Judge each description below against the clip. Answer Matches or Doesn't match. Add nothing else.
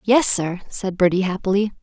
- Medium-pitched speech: Doesn't match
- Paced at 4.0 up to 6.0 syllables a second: Matches